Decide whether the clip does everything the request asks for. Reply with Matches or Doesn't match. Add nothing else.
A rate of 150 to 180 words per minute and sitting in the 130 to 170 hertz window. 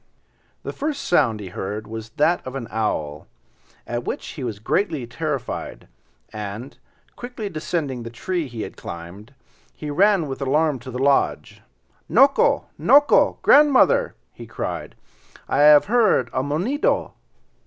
Doesn't match